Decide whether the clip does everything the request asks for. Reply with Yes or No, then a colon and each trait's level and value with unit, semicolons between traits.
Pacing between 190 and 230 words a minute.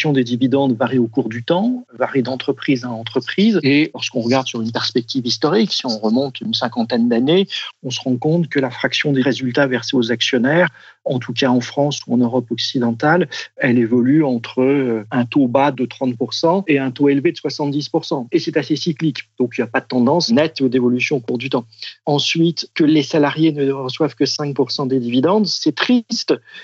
Yes: average, 200 wpm